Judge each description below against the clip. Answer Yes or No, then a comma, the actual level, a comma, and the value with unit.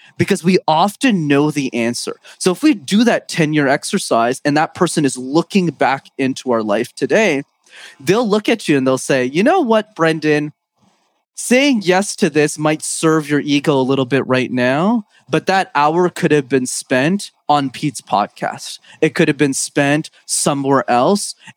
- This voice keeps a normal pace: Yes, average, 180 wpm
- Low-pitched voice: No, medium, 155 Hz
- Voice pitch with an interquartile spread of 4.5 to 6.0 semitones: Yes, average, 5.1 semitones